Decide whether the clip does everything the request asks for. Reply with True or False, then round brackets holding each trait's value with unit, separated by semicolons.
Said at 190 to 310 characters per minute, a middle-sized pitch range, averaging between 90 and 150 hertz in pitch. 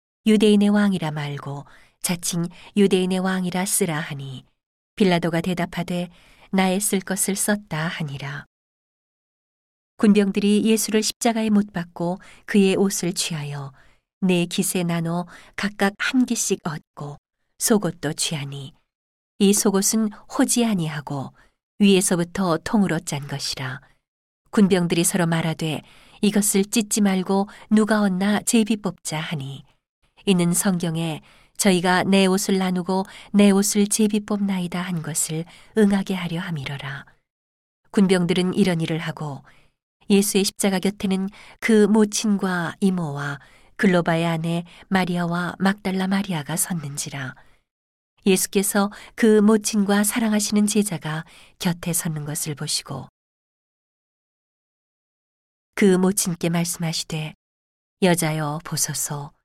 False (250 characters per minute; 3.9 semitones; 185 Hz)